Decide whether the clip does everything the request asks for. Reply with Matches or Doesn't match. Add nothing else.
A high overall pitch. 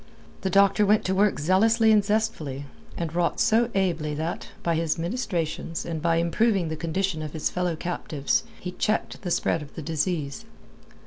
Doesn't match